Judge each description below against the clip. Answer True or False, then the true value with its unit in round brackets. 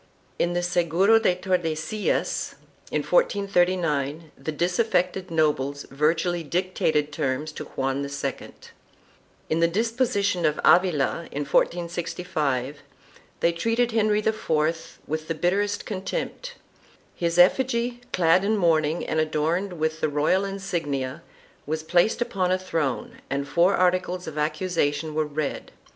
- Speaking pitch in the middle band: True (170 Hz)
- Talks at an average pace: False (125 wpm)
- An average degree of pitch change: True (3.6 semitones)